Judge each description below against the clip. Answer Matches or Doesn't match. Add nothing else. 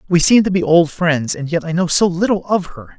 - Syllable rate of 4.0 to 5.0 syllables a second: Doesn't match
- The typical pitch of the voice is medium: Matches